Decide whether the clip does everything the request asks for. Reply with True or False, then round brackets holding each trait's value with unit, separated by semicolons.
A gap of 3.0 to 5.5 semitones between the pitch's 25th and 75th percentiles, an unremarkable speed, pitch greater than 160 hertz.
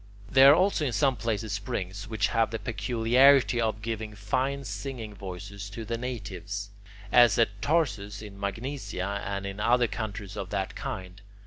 False (3.4 semitones; 160 wpm; 110 Hz)